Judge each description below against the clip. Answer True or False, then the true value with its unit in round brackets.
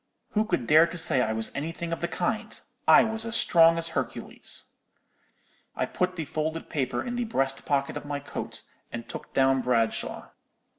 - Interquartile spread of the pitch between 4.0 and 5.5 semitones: True (4.3 semitones)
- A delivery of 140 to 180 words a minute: False (190 wpm)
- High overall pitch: False (155 Hz)